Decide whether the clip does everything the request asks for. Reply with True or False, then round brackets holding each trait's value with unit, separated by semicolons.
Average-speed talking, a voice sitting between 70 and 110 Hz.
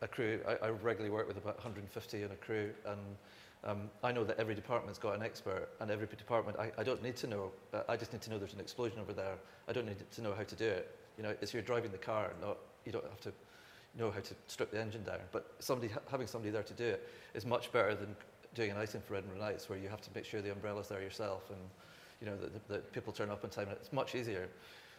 False (270 wpm; 105 Hz)